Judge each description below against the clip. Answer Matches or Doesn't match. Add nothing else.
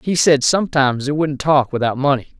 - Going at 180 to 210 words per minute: Matches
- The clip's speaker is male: Matches